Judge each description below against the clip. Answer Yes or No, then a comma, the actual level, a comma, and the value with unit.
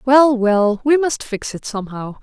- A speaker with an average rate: Yes, average, 190 wpm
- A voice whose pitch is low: No, high, 240 Hz